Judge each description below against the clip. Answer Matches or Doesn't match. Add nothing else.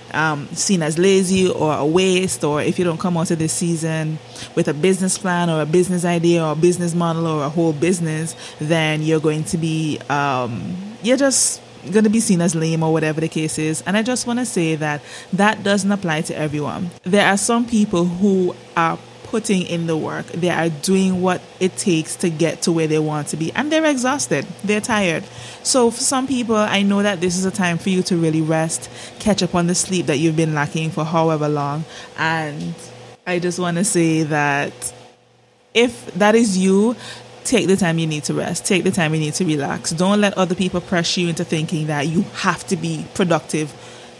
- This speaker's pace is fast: Matches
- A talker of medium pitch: Matches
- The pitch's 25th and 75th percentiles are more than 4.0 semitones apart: Doesn't match